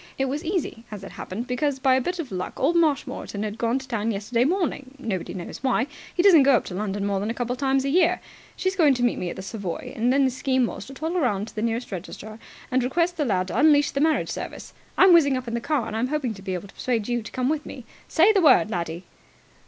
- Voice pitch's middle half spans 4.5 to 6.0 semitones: Yes, average, 5.2 semitones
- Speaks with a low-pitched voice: No, very high, 250 Hz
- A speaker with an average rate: No, fast, 270 wpm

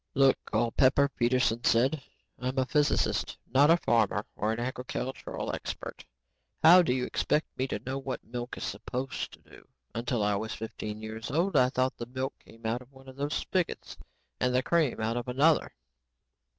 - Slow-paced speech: No, average, 180 wpm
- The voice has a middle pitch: No, low, 130 Hz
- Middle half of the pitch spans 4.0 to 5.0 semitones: No, average, 2.7 semitones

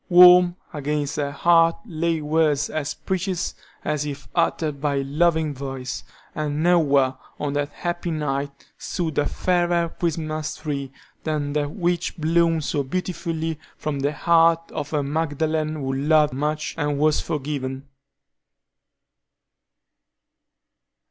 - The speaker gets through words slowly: Yes, slow, 125 wpm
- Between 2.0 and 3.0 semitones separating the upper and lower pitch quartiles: Yes, narrow, 2.6 semitones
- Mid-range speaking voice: Yes, medium, 155 Hz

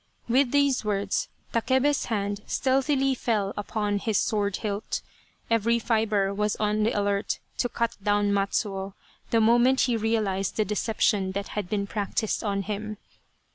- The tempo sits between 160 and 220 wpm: No, average, 145 wpm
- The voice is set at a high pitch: Yes, high, 210 Hz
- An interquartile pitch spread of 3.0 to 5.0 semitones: No, narrow, 2.5 semitones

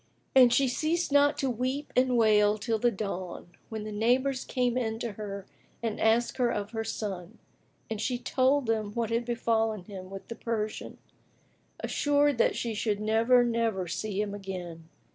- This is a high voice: Yes, high, 225 Hz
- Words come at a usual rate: Yes, average, 175 wpm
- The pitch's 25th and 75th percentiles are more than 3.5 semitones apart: No, average, 3.0 semitones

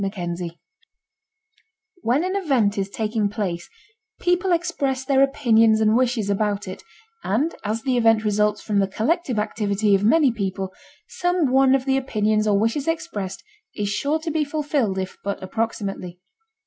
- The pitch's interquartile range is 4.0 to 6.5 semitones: Yes, average, 5.2 semitones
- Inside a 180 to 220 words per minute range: No, average, 160 wpm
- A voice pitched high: Yes, high, 220 Hz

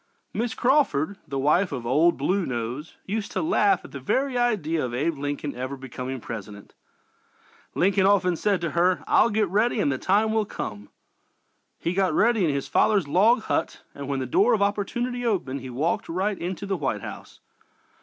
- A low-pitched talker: No, medium, 180 Hz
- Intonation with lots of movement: Yes, wide, 7.2 semitones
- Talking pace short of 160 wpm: No, average, 185 wpm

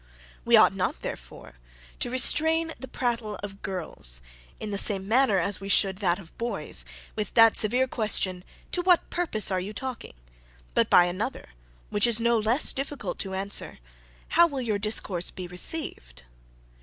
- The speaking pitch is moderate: No, high, 210 Hz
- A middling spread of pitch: Yes, average, 4.9 semitones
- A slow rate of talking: No, average, 165 wpm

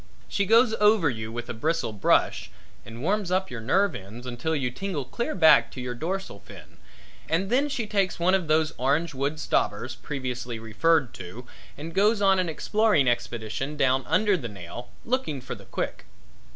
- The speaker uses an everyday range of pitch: No, wide, 7.9 semitones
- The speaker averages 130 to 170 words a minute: No, average, 180 wpm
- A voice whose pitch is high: No, medium, 155 Hz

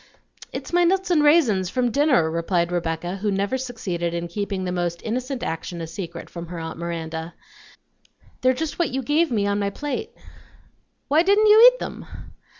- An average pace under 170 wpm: No, average, 180 wpm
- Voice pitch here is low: No, high, 200 Hz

